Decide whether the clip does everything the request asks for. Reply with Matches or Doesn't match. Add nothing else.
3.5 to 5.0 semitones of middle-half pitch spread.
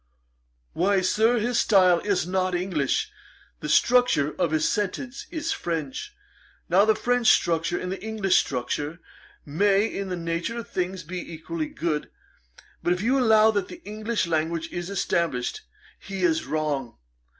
Matches